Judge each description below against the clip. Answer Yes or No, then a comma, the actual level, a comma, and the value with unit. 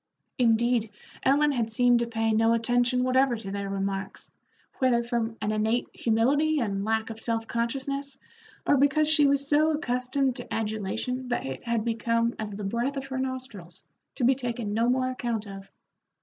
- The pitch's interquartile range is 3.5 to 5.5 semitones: No, average, 2.8 semitones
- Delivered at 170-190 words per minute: Yes, average, 175 wpm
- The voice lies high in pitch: Yes, high, 235 Hz